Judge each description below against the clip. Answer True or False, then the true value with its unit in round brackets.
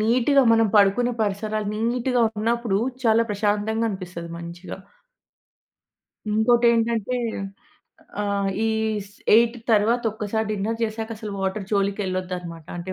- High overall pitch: True (215 Hz)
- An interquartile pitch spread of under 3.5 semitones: True (2.7 semitones)